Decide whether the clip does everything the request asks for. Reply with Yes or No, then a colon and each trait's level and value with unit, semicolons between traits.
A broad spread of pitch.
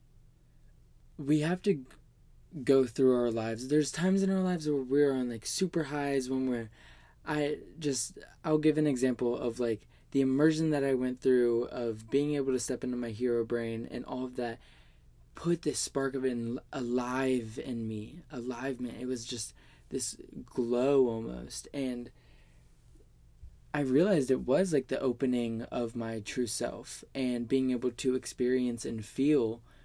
No: average, 3.0 semitones